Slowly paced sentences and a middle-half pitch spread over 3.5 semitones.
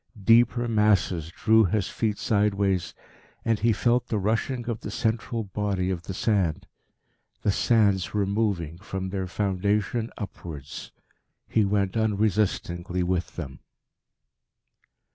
No: slow, 125 wpm; average, 3.1 semitones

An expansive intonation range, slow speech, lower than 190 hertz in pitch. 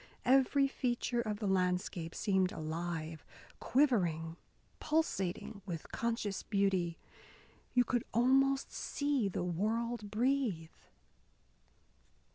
No: wide, 6.0 semitones; slow, 90 wpm; high, 210 Hz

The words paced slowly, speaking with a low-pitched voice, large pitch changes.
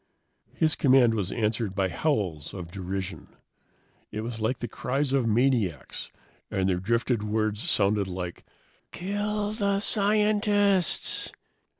Yes: slow, 120 wpm; low, 115 Hz; wide, 8.9 semitones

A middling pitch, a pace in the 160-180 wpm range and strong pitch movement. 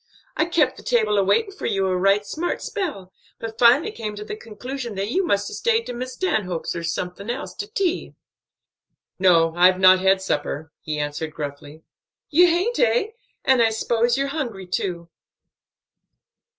No: high, 215 Hz; average, 175 wpm; wide, 7.0 semitones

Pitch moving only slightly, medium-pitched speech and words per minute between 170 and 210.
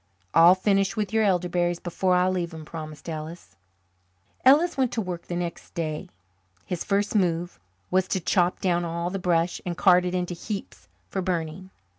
Yes: narrow, 1.9 semitones; medium, 180 Hz; average, 175 wpm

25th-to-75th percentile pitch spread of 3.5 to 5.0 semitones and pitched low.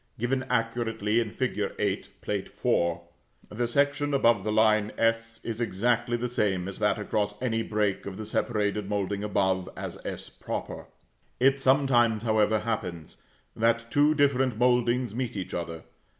No: average, 2.8 semitones; low, 115 Hz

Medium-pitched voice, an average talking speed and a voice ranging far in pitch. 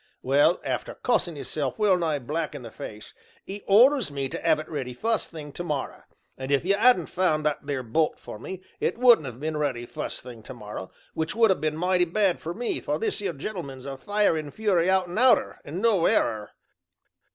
No: medium, 160 Hz; fast, 215 wpm; wide, 5.7 semitones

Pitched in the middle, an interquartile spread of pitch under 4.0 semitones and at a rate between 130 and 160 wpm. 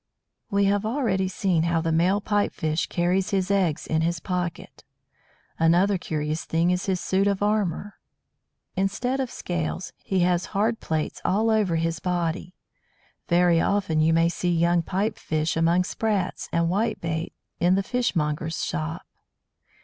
Yes: medium, 180 Hz; average, 3.3 semitones; average, 150 wpm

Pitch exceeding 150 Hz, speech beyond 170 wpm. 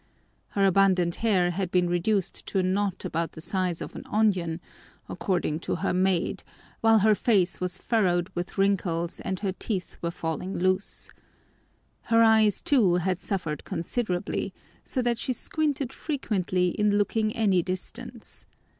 No: high, 190 Hz; average, 150 wpm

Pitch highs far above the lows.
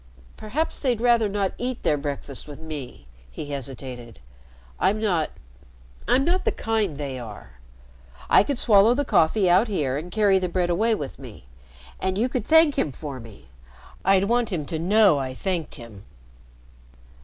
Yes: wide, 7.8 semitones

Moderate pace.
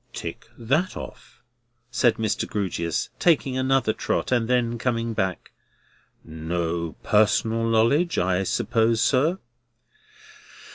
No: slow, 105 wpm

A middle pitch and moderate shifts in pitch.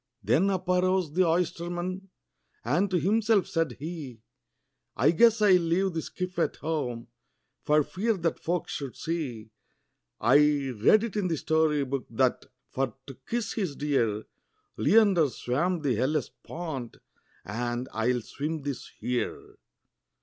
No: medium, 160 Hz; wide, 5.8 semitones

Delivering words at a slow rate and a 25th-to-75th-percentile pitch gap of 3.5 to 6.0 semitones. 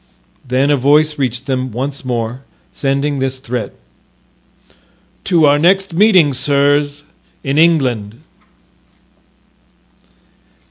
No: slow, 95 wpm; narrow, 2.6 semitones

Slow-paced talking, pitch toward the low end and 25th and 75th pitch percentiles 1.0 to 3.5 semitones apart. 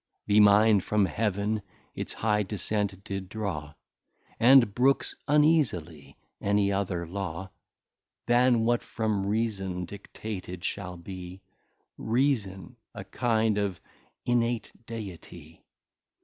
Yes: slow, 105 wpm; low, 100 Hz; average, 3.2 semitones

